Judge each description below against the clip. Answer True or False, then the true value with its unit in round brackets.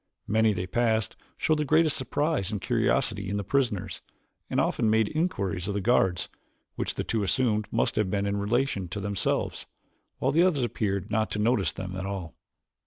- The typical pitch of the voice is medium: False (105 Hz)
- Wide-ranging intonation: False (4.2 semitones)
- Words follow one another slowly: False (180 wpm)